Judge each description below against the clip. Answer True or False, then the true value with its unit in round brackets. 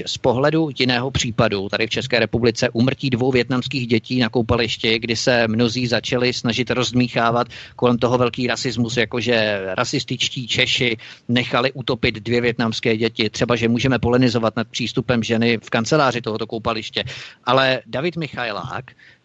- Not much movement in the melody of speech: True (1.5 semitones)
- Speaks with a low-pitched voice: True (120 Hz)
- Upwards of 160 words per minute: False (145 wpm)